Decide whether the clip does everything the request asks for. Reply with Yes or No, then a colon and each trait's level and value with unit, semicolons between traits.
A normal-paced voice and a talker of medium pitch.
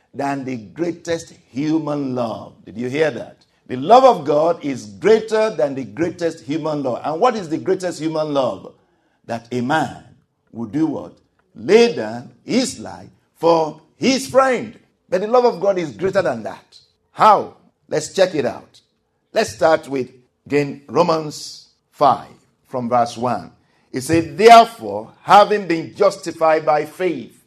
Yes: average, 155 wpm; medium, 160 Hz